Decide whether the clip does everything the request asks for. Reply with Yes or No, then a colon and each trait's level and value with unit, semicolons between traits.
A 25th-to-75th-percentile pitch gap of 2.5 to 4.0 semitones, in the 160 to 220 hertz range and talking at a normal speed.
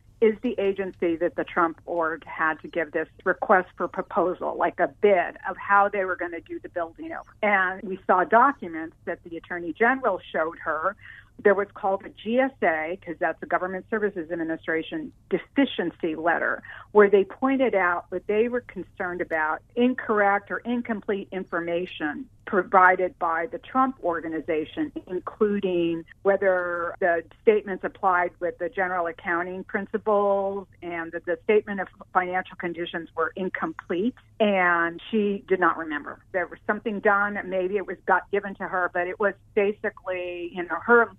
Yes: average, 3.1 semitones; medium, 185 Hz; average, 160 wpm